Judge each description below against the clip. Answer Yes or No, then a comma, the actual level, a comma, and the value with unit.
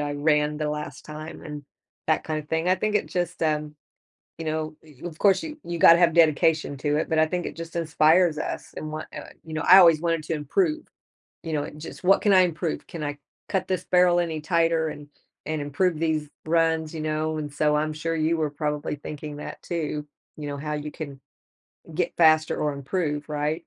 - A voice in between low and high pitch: Yes, medium, 155 Hz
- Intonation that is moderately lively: No, narrow, 1.8 semitones